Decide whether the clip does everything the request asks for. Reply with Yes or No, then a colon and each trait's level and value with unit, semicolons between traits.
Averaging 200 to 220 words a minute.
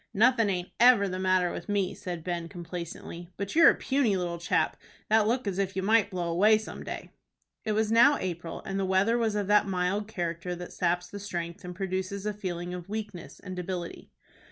Yes: fast, 205 wpm